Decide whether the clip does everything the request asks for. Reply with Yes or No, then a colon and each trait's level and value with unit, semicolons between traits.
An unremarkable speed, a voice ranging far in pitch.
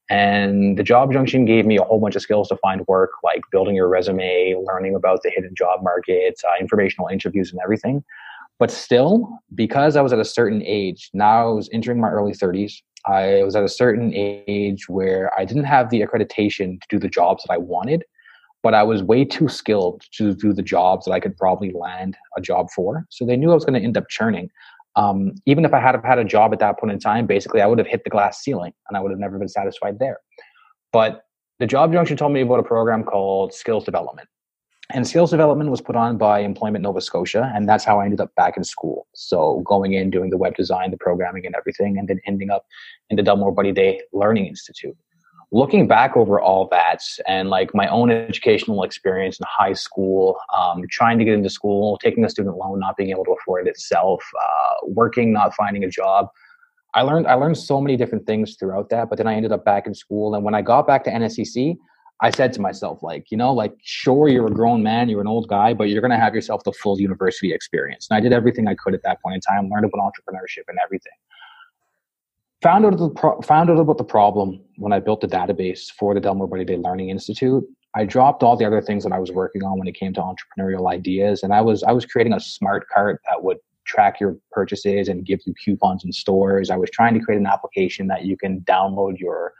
No: fast, 235 wpm; wide, 5.9 semitones